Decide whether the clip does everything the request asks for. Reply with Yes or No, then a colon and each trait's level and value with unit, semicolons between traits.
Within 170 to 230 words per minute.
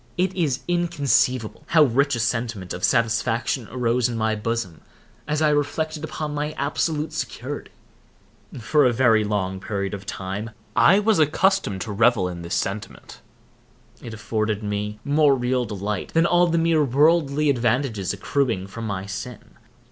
No: average, 155 wpm